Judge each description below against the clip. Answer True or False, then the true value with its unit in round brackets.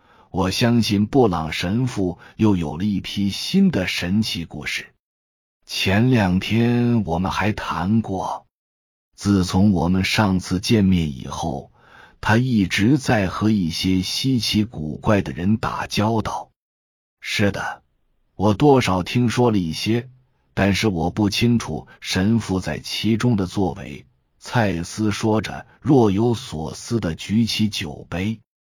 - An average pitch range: True (4.4 semitones)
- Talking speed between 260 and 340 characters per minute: False (185 characters per minute)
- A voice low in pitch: True (100 Hz)